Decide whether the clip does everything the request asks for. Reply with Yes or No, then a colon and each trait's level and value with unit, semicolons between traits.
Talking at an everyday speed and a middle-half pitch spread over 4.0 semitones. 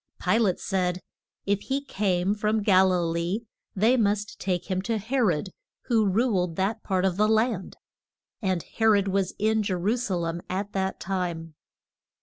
No: average, 175 wpm; average, 2.9 semitones